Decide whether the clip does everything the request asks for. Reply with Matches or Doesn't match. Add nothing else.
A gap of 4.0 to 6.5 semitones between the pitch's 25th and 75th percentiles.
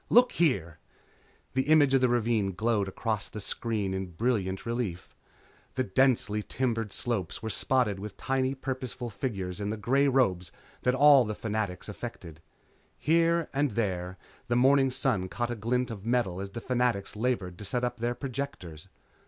Matches